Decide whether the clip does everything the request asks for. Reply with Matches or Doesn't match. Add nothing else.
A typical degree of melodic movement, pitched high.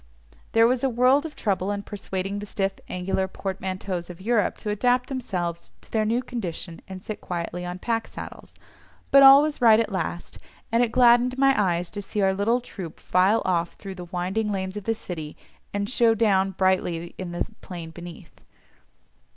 Matches